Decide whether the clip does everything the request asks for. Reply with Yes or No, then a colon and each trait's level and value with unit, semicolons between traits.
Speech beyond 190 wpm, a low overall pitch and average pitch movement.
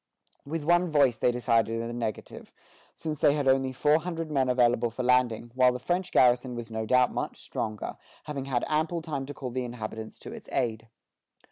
Yes: average, 200 wpm; low, 125 Hz; average, 3.8 semitones